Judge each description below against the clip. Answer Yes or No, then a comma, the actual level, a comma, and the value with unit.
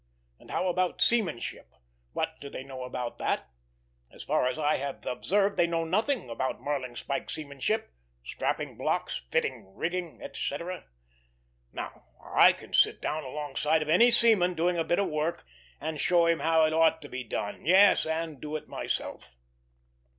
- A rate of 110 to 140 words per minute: No, average, 165 wpm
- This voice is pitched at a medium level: Yes, medium, 160 Hz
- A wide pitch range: No, average, 4.0 semitones